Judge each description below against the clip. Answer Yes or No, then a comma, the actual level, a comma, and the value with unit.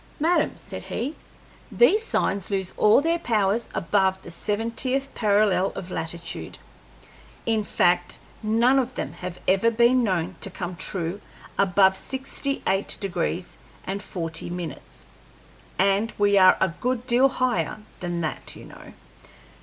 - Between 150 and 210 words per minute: No, average, 140 wpm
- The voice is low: No, high, 200 Hz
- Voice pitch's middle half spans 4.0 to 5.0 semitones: Yes, average, 4.7 semitones